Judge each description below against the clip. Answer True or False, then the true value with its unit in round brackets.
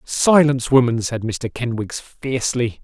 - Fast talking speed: False (125 wpm)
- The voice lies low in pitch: True (125 Hz)